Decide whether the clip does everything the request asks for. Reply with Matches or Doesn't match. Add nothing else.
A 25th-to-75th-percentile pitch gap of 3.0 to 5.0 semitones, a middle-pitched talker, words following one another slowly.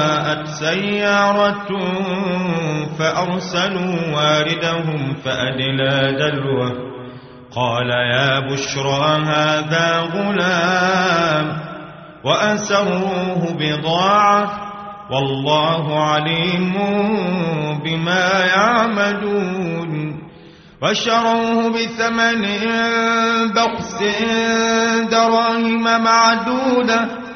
Doesn't match